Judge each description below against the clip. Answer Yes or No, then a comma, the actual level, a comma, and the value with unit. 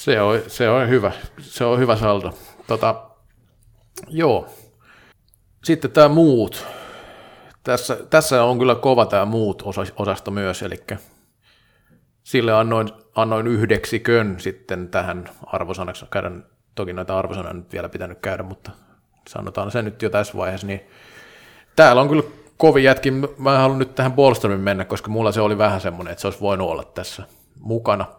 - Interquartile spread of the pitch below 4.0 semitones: No, average, 4.3 semitones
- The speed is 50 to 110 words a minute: No, average, 150 wpm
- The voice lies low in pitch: Yes, low, 110 Hz